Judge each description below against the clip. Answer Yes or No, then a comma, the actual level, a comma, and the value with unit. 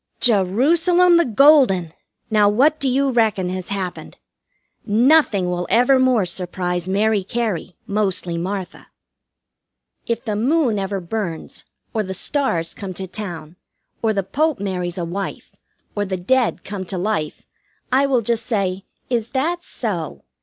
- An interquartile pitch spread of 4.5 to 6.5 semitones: Yes, average, 5.3 semitones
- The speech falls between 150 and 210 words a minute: No, average, 140 wpm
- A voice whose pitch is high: Yes, high, 205 Hz